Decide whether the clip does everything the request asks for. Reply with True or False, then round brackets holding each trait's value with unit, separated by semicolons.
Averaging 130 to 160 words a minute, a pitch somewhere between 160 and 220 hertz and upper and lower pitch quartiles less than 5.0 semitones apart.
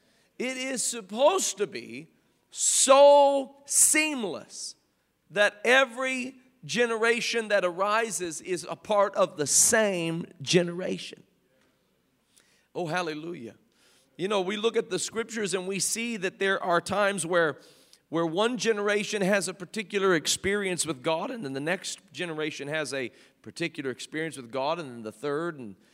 False (140 wpm; 190 Hz; 5.6 semitones)